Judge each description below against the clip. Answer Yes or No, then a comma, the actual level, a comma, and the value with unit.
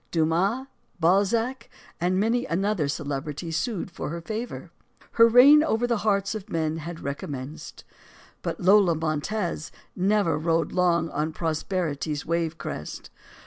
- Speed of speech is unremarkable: No, slow, 130 wpm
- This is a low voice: No, medium, 170 Hz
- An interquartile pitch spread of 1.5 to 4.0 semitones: No, average, 5.0 semitones